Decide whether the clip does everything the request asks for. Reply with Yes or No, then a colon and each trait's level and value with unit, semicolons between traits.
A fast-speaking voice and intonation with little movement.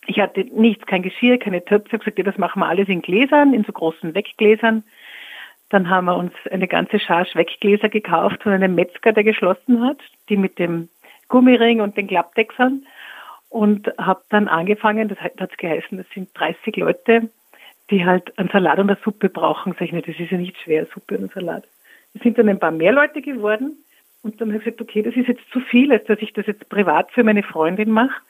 No: fast, 215 wpm; average, 3.6 semitones